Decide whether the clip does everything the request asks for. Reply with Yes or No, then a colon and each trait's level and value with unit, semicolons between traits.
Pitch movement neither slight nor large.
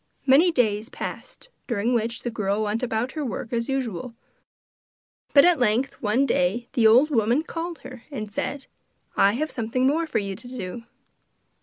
Yes: average, 3.9 semitones